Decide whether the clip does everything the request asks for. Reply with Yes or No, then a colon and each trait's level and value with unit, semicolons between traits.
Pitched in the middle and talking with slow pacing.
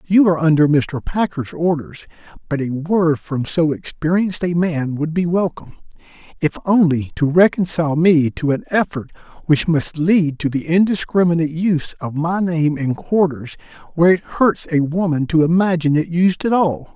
No: medium, 160 Hz; average, 170 wpm